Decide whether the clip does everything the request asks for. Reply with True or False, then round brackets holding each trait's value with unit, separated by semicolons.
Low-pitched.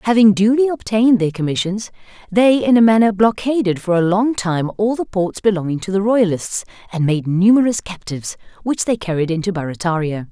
False (200 Hz)